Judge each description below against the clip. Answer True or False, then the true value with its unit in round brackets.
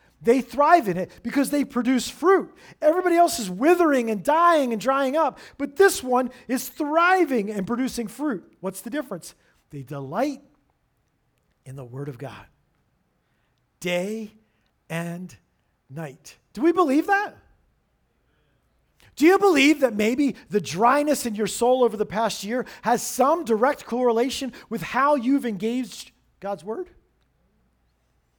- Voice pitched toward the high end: True (245 Hz)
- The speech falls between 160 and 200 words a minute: False (140 wpm)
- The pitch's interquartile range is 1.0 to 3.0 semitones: False (5.6 semitones)